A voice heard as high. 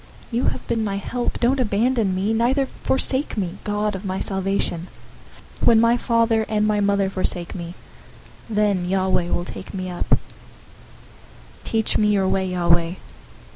Yes: high, 200 Hz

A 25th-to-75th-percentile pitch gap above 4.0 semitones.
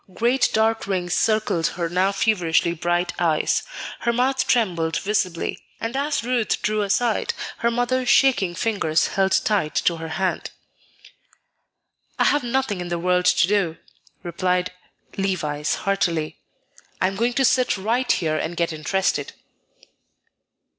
Yes: average, 5.1 semitones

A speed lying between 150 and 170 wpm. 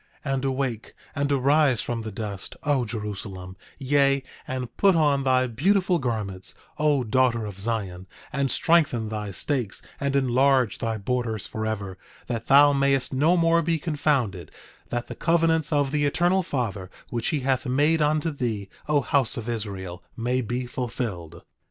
Yes: average, 160 wpm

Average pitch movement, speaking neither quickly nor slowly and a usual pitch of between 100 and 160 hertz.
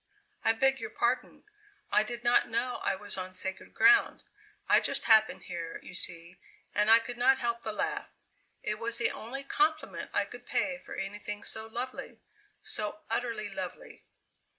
No: average, 3.1 semitones; average, 170 wpm; high, 225 Hz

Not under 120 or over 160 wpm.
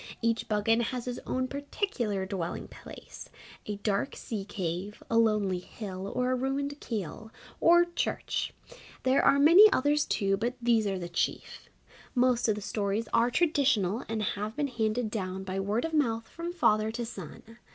No: average, 170 wpm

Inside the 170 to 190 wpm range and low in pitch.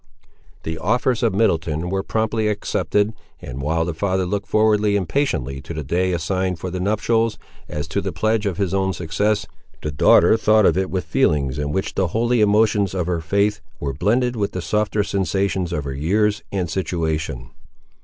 Yes: average, 185 wpm; very low, 95 Hz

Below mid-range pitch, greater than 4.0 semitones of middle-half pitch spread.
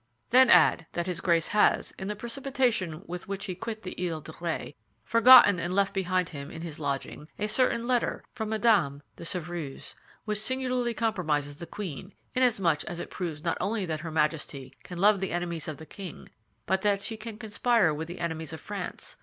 No: medium, 185 Hz; average, 5.1 semitones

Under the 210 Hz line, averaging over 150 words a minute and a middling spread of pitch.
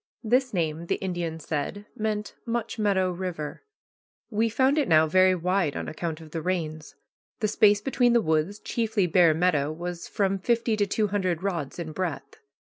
Yes: medium, 185 Hz; average, 175 wpm; average, 4.6 semitones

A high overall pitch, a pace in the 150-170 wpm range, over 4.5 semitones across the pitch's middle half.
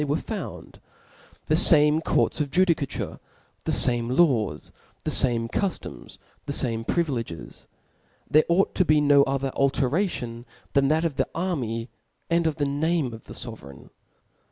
No: medium, 140 Hz; average, 155 wpm; average, 5.1 semitones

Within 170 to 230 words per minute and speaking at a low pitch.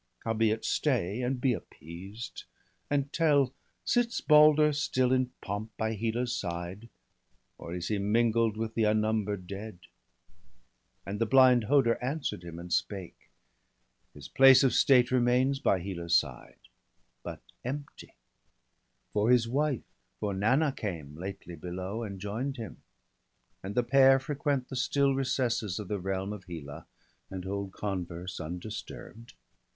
No: average, 140 wpm; low, 110 Hz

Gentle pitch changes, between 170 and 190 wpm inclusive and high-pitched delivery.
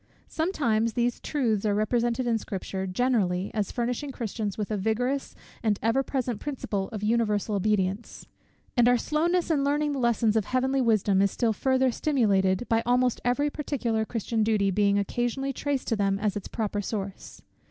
No: average, 3.8 semitones; average, 175 wpm; high, 230 Hz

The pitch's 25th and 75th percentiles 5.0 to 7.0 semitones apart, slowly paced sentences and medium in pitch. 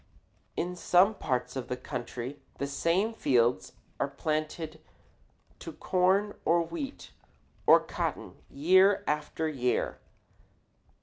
Yes: wide, 5.6 semitones; slow, 110 wpm; medium, 155 Hz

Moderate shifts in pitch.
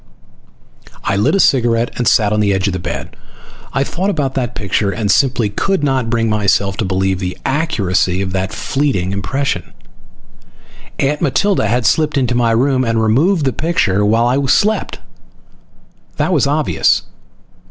No: wide, 5.7 semitones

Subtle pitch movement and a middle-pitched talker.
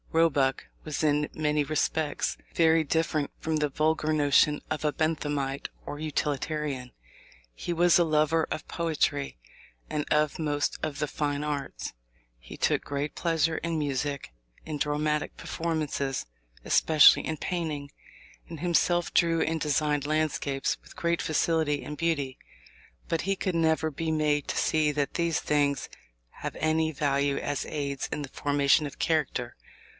Yes: narrow, 1.8 semitones; medium, 150 Hz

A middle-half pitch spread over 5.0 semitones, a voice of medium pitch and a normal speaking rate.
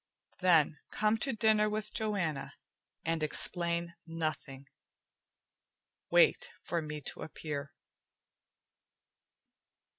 No: wide, 5.5 semitones; medium, 170 Hz; slow, 85 wpm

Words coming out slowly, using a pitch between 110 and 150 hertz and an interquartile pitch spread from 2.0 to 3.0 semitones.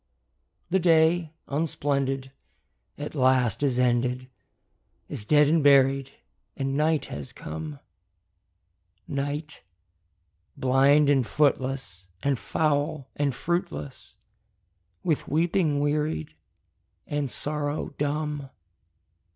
Yes: slow, 90 wpm; medium, 140 Hz; narrow, 2.6 semitones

